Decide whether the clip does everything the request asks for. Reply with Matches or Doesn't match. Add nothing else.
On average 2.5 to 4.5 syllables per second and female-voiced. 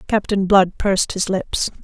Matches